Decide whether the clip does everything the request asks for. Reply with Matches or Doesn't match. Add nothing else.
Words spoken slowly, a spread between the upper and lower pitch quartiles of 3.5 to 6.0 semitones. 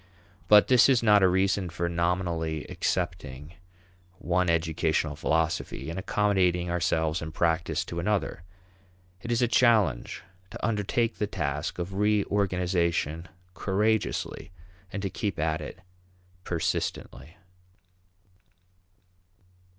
Matches